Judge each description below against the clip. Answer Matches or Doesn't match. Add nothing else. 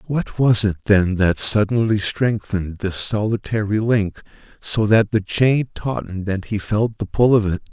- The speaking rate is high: Doesn't match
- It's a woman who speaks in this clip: Doesn't match